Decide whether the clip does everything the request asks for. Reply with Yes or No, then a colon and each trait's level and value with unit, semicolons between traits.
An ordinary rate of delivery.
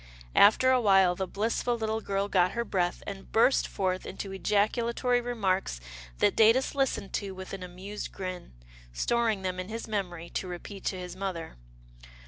Yes: average, 165 wpm